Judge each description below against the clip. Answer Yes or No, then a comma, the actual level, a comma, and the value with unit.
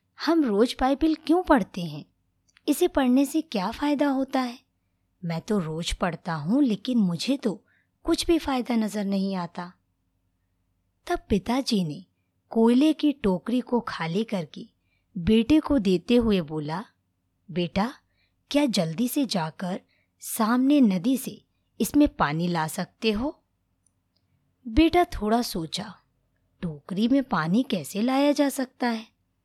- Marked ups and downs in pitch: Yes, wide, 7.9 semitones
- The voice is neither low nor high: No, high, 215 Hz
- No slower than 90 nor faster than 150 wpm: Yes, average, 130 wpm